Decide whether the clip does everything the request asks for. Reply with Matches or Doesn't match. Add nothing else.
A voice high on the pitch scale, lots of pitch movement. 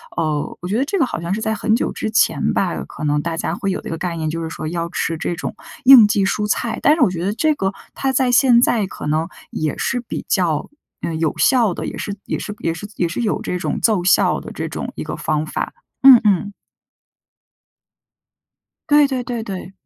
Matches